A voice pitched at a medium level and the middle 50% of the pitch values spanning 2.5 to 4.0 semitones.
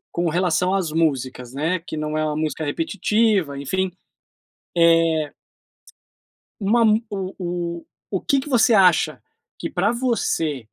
No: medium, 170 Hz; average, 4.6 semitones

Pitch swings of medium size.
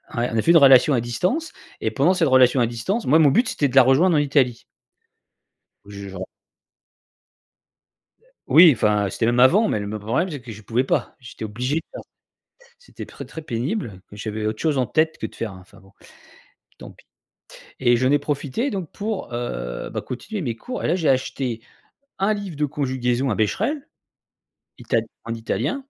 No: wide, 6.1 semitones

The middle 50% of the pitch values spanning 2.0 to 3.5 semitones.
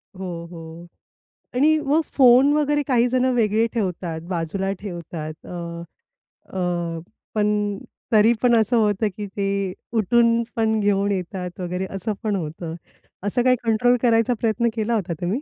No: average, 4.4 semitones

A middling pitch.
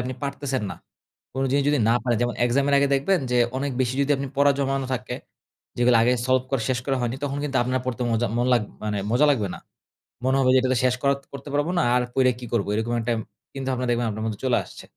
No: low, 130 Hz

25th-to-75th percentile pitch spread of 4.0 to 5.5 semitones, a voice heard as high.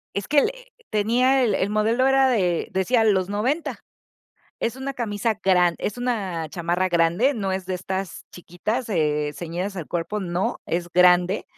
Yes: average, 4.7 semitones; high, 195 Hz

